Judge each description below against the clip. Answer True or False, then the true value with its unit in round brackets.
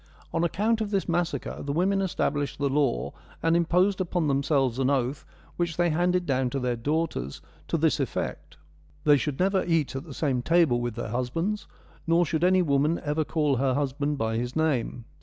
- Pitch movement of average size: True (4.4 semitones)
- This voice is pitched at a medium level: True (150 Hz)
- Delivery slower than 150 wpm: False (190 wpm)